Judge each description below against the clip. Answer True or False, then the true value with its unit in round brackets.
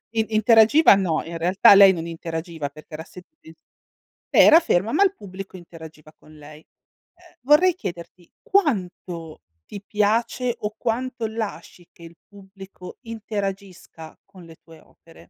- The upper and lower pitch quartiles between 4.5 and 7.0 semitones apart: True (5.1 semitones)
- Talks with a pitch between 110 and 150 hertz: False (195 Hz)